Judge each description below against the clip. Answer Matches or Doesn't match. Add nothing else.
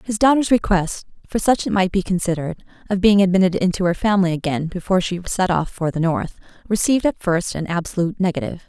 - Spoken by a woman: Matches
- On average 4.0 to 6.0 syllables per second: Doesn't match